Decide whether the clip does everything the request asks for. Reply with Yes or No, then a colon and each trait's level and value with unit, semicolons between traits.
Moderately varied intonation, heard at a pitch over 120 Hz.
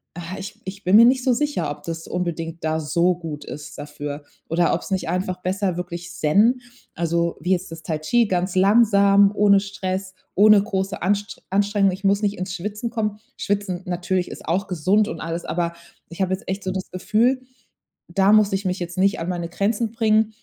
Yes: average, 3.0 semitones; high, 190 Hz